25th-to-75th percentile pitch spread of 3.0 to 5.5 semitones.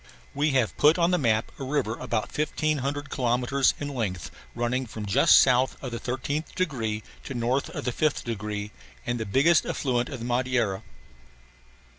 Yes: average, 3.8 semitones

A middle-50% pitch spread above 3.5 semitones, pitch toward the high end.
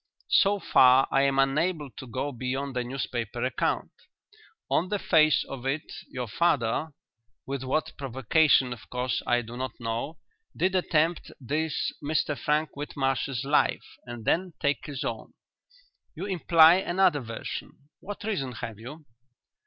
No: average, 4.0 semitones; medium, 140 Hz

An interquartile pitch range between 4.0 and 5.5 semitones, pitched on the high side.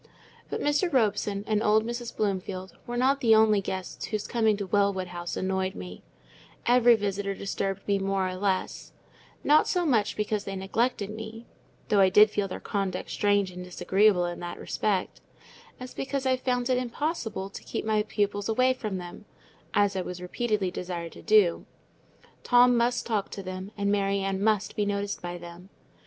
No: average, 3.0 semitones; high, 205 Hz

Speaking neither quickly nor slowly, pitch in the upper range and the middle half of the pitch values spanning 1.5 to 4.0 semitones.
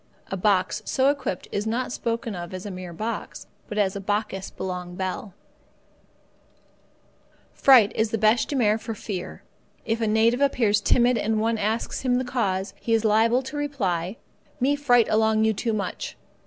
Yes: average, 180 wpm; high, 220 Hz; average, 3.2 semitones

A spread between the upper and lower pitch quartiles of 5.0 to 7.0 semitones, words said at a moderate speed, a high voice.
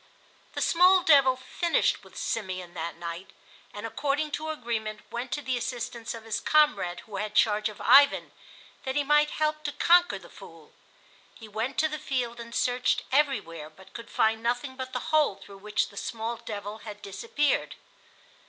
Yes: wide, 5.4 semitones; average, 175 wpm; high, 235 Hz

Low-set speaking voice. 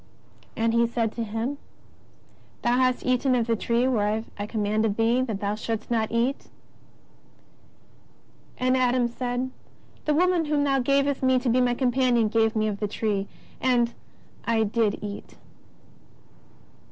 No: high, 235 Hz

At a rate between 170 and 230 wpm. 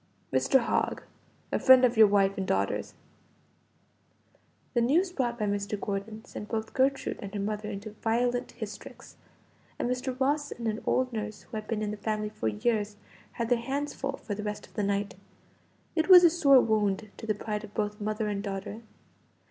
Yes: average, 190 wpm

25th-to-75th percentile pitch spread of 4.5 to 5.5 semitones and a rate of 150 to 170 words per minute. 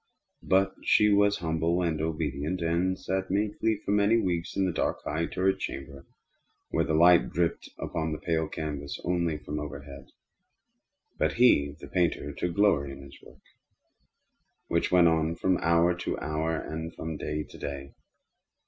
No: average, 3.2 semitones; average, 160 wpm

